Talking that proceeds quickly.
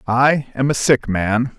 No: average, 190 wpm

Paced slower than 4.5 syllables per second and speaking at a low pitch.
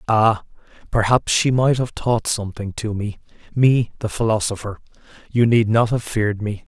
No: 5.0 syllables/s; low, 110 Hz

